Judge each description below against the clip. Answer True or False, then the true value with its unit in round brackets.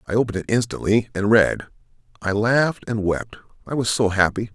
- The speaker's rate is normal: True (185 wpm)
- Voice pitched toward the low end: True (105 Hz)